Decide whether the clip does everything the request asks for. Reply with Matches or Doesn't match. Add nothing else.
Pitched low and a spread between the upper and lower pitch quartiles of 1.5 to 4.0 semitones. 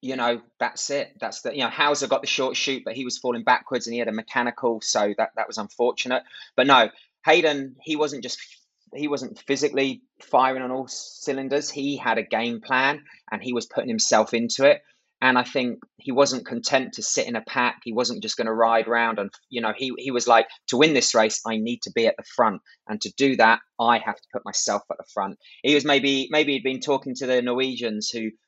Matches